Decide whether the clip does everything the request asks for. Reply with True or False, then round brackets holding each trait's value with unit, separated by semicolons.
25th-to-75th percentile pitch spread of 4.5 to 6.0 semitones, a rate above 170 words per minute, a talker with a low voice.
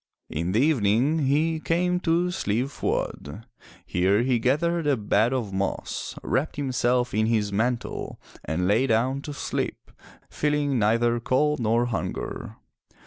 False (5.2 semitones; 140 wpm; 125 Hz)